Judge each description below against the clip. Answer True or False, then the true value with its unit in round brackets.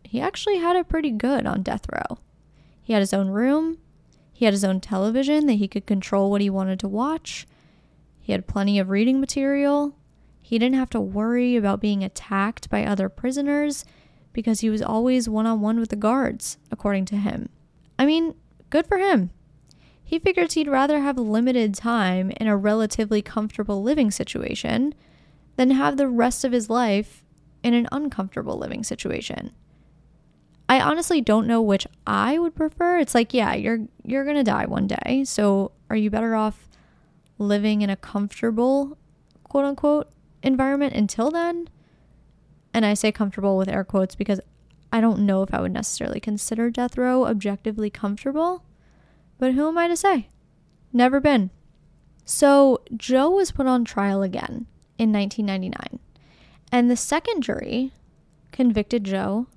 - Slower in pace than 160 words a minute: False (165 wpm)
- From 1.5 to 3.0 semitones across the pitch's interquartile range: False (4.9 semitones)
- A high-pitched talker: True (230 Hz)